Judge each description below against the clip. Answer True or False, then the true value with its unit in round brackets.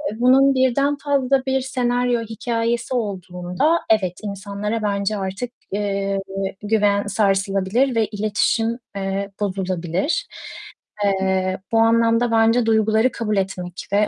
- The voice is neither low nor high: False (215 Hz)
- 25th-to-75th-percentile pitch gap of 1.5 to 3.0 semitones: False (3.6 semitones)